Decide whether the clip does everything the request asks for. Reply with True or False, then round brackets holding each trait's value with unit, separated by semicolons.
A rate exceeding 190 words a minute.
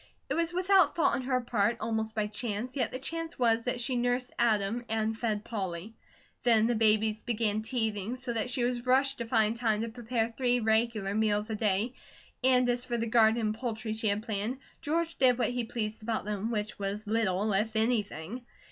True (200 wpm)